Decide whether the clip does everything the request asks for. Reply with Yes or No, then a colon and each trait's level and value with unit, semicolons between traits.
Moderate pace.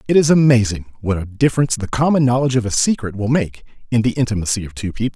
No: fast, 235 wpm